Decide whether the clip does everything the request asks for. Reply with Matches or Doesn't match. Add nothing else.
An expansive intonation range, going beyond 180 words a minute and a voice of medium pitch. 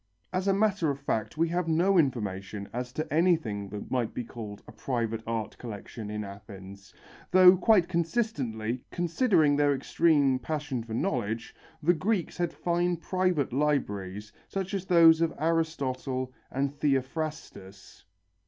Doesn't match